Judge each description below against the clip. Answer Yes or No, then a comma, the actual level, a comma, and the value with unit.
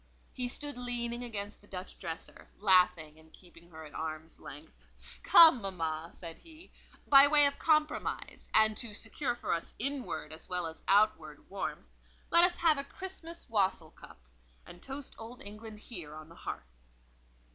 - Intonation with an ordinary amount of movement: No, wide, 8.6 semitones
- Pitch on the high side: Yes, high, 210 Hz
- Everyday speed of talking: Yes, average, 165 wpm